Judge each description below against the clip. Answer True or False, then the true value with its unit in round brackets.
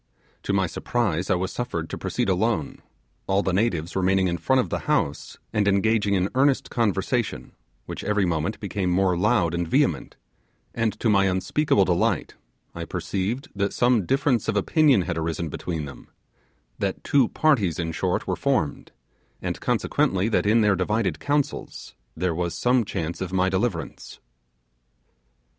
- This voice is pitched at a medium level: False (95 Hz)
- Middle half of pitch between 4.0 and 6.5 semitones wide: True (4.3 semitones)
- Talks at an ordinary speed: True (160 wpm)